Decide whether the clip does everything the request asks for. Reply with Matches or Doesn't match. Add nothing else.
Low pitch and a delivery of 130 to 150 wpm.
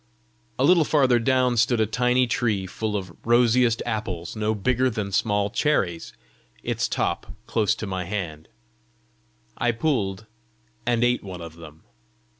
Matches